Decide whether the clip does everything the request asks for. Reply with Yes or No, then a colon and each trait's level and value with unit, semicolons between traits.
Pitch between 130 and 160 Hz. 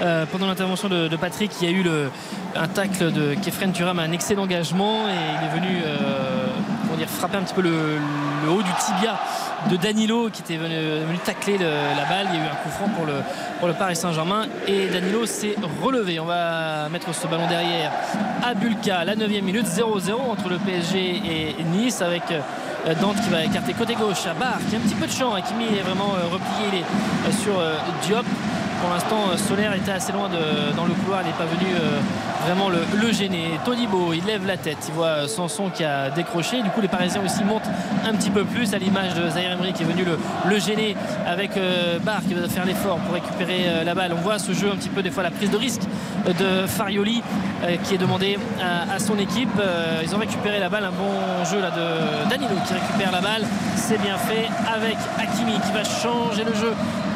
No: high, 195 Hz